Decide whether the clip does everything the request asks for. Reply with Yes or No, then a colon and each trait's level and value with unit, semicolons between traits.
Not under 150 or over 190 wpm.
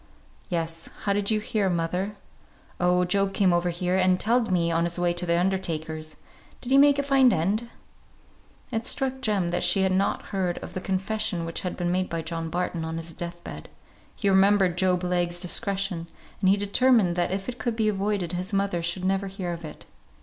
No: fast, 205 wpm